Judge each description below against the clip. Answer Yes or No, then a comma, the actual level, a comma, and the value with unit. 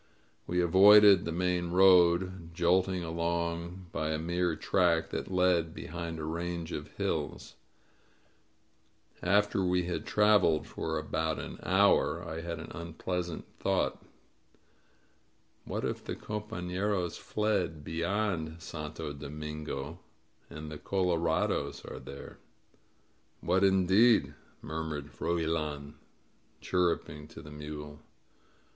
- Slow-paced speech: Yes, slow, 110 wpm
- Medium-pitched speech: No, very low, 85 Hz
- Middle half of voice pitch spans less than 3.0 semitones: Yes, narrow, 2.5 semitones